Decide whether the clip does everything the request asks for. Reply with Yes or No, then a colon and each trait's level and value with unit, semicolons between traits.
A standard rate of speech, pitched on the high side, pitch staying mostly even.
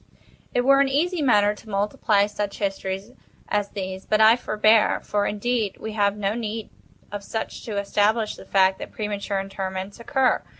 Yes: average, 160 wpm; high, 210 Hz; narrow, 2.0 semitones